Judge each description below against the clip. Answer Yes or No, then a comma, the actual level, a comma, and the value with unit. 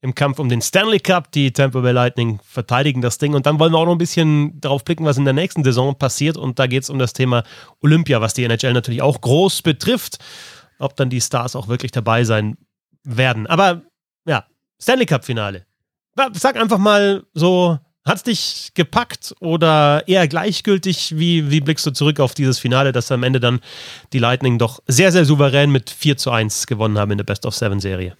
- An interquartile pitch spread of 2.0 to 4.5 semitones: No, average, 5.0 semitones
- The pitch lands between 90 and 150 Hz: Yes, medium, 140 Hz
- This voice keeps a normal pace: No, fast, 205 wpm